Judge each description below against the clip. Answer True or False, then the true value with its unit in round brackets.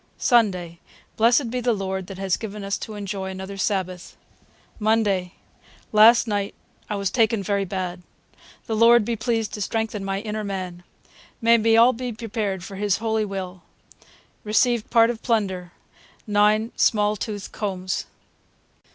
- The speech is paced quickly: False (150 wpm)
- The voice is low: False (210 Hz)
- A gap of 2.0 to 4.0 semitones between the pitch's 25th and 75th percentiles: True (2.8 semitones)